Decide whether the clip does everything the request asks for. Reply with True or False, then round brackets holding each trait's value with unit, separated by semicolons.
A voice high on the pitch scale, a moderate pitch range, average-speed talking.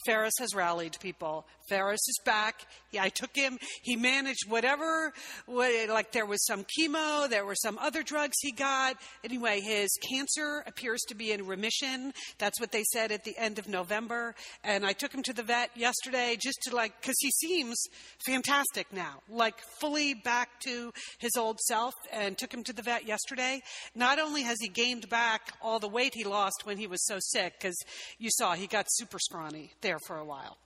True (235 Hz; 4.0 semitones; 195 wpm)